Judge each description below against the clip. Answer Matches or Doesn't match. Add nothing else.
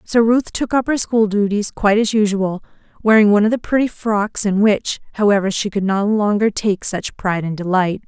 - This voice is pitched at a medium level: Doesn't match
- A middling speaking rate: Doesn't match